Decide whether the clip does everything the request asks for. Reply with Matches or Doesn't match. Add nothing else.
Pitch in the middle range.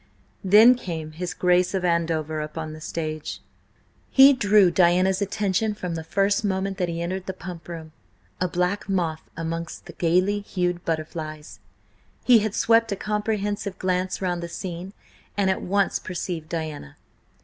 Matches